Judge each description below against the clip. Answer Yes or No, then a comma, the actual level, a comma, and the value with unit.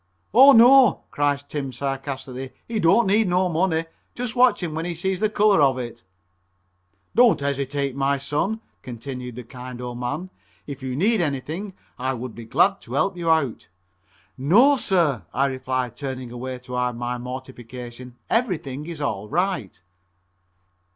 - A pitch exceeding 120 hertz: Yes, medium, 140 Hz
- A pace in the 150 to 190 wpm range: Yes, average, 155 wpm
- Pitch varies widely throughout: Yes, wide, 6.6 semitones